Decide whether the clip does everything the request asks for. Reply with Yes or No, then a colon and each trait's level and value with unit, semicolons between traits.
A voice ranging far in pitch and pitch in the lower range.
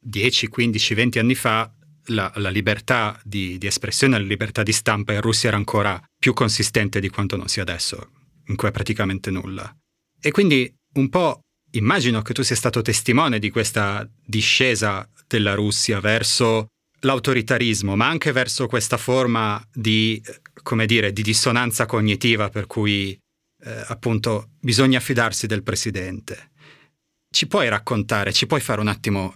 No: average, 3.1 semitones; low, 110 Hz